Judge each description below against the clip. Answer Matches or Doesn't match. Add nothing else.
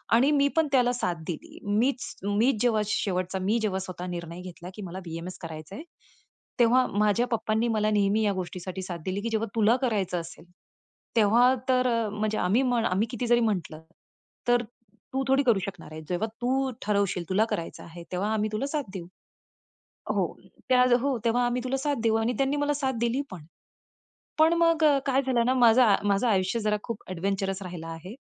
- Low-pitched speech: Doesn't match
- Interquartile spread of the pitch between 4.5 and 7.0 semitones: Matches